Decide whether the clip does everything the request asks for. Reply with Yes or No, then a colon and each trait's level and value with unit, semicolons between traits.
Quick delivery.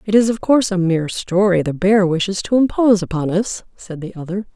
Yes: fast, 225 wpm